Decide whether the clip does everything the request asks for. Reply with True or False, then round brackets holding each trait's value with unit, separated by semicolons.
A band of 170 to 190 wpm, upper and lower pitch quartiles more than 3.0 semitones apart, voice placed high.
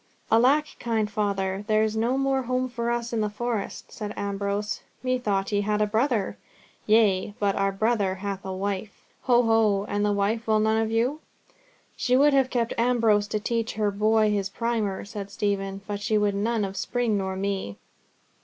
False (185 wpm; 2.6 semitones; 215 Hz)